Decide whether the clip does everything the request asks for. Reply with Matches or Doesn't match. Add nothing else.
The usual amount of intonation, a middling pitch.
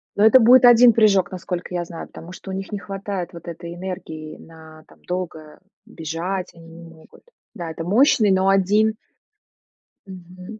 Matches